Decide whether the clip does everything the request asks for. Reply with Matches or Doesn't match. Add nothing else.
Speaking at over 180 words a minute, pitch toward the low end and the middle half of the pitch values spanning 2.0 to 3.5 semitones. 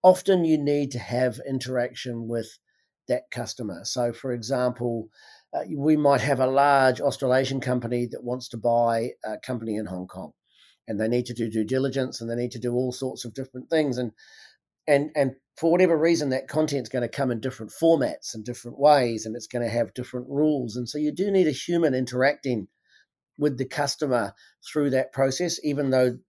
Matches